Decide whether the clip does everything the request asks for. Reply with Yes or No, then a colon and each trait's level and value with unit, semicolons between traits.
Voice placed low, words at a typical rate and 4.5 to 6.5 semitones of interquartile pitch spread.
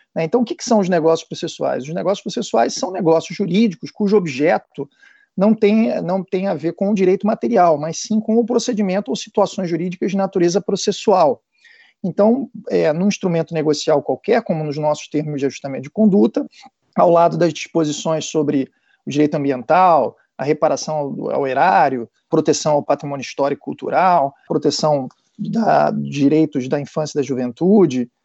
No: medium, 175 Hz; average, 165 wpm; wide, 5.5 semitones